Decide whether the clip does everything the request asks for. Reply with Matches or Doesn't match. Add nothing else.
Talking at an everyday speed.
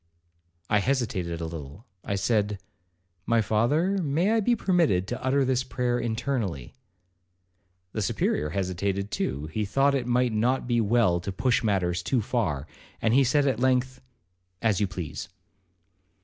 Matches